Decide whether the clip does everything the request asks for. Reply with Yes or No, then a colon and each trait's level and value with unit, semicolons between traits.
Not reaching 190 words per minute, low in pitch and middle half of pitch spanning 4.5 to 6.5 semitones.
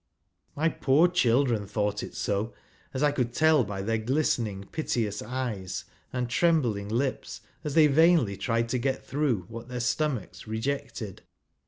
Yes: average, 150 wpm; low, 125 Hz; average, 4.8 semitones